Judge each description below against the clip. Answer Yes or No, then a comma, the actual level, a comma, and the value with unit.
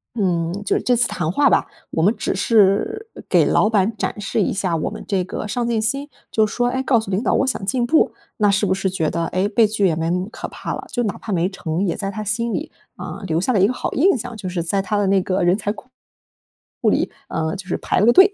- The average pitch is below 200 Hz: No, high, 205 Hz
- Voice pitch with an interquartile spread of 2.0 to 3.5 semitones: No, average, 4.1 semitones